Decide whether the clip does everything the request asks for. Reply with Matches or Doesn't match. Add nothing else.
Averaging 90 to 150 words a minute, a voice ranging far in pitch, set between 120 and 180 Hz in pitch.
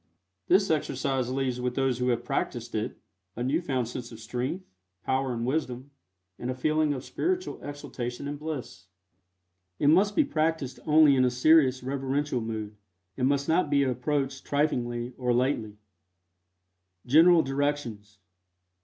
Doesn't match